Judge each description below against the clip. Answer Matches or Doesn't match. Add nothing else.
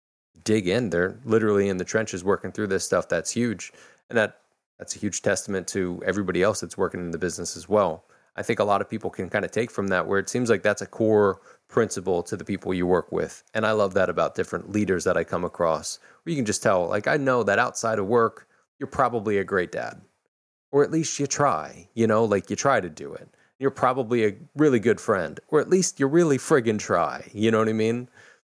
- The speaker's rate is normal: Doesn't match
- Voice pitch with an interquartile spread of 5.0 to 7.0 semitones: Doesn't match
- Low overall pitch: Matches